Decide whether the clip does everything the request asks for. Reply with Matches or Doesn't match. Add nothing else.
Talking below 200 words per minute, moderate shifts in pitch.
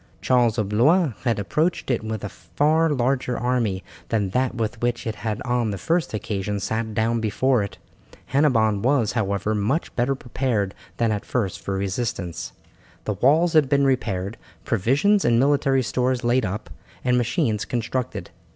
Matches